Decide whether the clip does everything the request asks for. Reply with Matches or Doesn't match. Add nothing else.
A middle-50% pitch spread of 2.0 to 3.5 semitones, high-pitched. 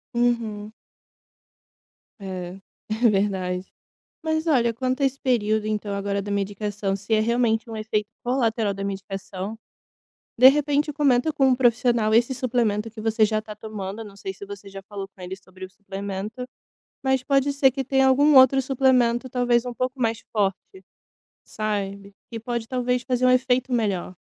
Doesn't match